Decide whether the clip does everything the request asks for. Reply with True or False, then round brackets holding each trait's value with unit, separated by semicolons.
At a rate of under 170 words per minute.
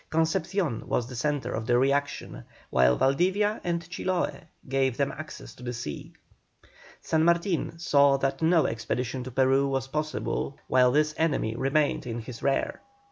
True (155 wpm)